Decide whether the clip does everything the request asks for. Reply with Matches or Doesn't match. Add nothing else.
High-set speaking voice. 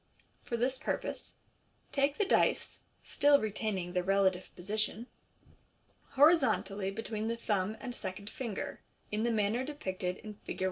Matches